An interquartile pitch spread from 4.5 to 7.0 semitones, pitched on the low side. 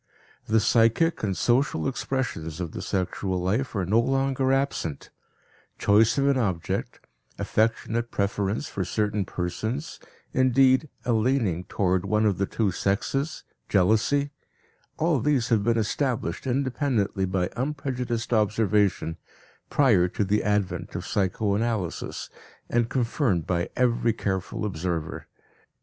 Yes: average, 5.2 semitones; low, 110 Hz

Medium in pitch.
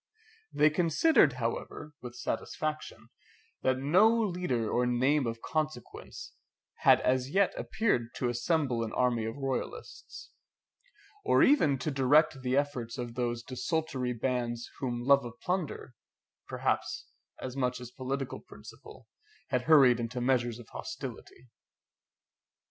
No: low, 130 Hz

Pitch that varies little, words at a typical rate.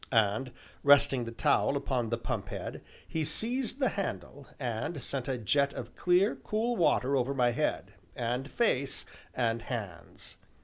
No: average, 5.1 semitones; average, 150 wpm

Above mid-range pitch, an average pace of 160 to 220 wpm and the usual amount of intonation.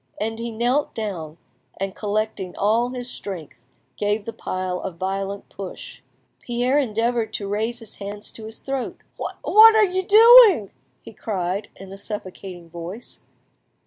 No: high, 215 Hz; average, 145 wpm; average, 3.9 semitones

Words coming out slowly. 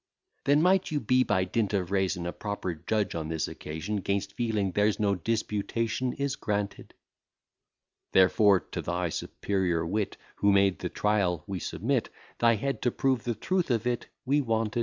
No: average, 170 wpm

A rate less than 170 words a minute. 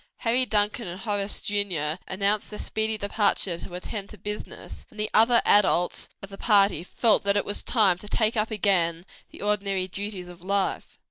No: average, 185 wpm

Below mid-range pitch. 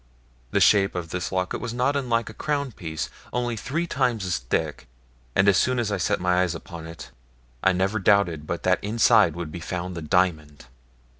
Yes: very low, 95 Hz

